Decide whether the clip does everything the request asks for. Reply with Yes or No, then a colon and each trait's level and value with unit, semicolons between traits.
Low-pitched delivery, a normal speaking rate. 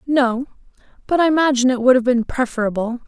No: very high, 255 Hz; average, 175 wpm